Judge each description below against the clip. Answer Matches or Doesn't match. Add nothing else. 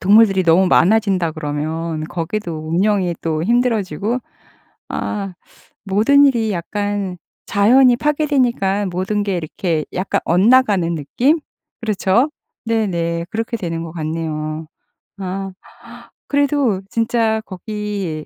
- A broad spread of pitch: Doesn't match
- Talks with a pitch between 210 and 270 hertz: Doesn't match